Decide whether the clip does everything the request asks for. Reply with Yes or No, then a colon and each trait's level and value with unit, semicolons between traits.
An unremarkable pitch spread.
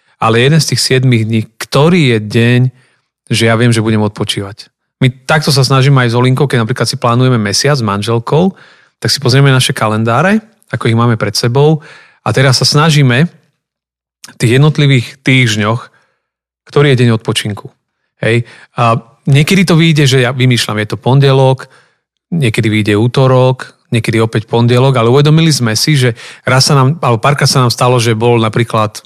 Yes: average, 3.4 semitones